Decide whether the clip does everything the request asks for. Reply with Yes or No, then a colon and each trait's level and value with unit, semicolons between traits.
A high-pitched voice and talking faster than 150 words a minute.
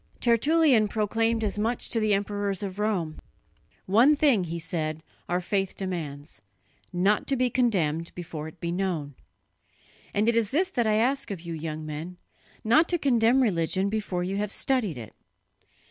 Yes: high, 200 Hz; average, 165 wpm